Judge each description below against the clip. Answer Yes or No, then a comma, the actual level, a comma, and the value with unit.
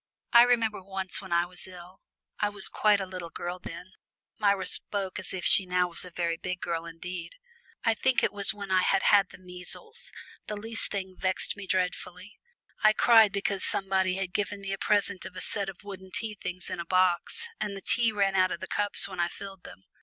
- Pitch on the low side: No, high, 190 Hz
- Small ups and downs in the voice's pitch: Yes, narrow, 2.1 semitones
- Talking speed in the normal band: No, fast, 220 wpm